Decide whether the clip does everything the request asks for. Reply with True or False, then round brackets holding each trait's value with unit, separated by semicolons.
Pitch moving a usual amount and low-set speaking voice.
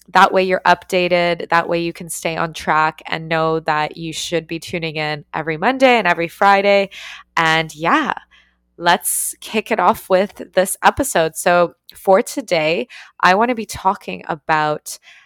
False (3.0 semitones; 175 Hz)